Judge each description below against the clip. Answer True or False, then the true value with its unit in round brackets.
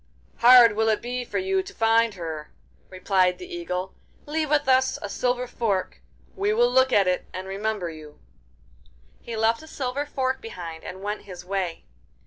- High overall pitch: True (225 Hz)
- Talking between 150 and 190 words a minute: True (175 wpm)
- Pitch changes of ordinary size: False (5.8 semitones)